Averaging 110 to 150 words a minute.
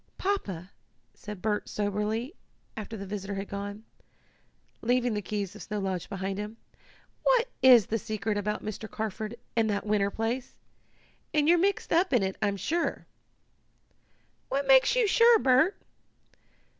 Yes: average, 145 wpm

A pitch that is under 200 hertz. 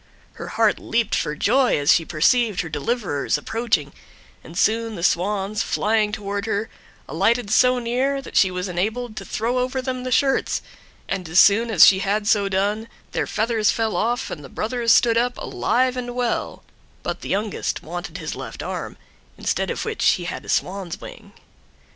No: high, 215 Hz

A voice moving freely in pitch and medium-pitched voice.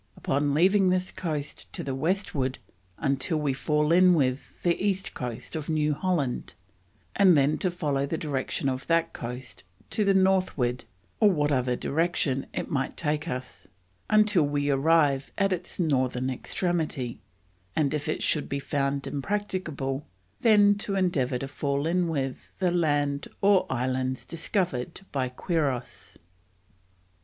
No: average, 4.8 semitones; medium, 150 Hz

